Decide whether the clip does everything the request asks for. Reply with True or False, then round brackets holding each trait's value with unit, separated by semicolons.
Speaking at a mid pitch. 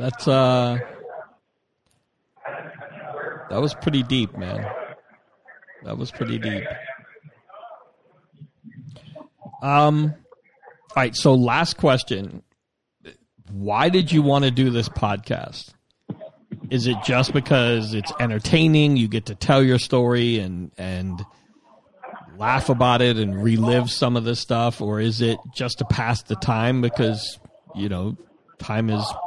False (125 Hz)